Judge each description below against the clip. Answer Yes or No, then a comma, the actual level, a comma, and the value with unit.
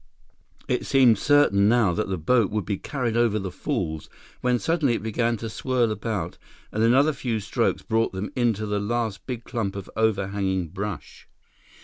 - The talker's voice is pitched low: Yes, low, 110 Hz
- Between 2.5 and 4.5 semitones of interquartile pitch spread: Yes, average, 3.2 semitones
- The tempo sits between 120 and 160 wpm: No, average, 170 wpm